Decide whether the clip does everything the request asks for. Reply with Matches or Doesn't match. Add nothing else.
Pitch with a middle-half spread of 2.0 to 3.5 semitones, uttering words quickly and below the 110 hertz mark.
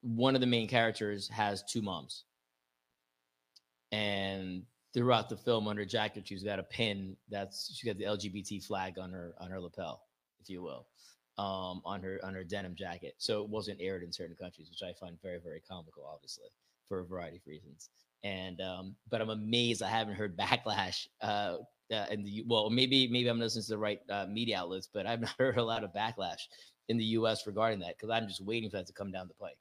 Matches